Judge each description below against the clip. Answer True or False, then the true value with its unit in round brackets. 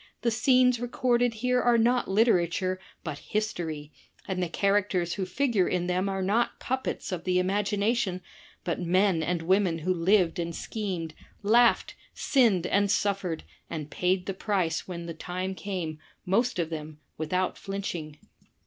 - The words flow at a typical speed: True (150 wpm)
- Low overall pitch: False (185 Hz)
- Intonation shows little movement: False (3.7 semitones)